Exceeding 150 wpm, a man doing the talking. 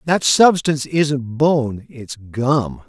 No: slow, 125 wpm; male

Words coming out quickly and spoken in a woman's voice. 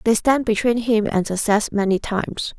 No: average, 185 wpm; female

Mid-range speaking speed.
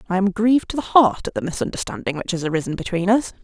No: fast, 245 wpm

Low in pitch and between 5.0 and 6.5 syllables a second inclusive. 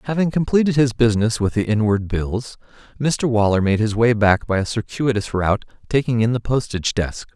Yes: low, 115 Hz; 5.5 syllables/s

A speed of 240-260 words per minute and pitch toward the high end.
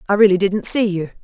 Yes: fast, 245 wpm; high, 195 Hz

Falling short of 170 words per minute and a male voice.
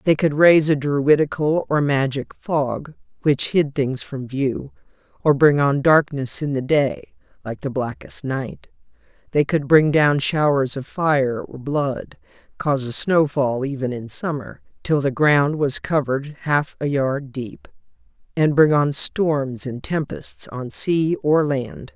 No: average, 160 wpm; female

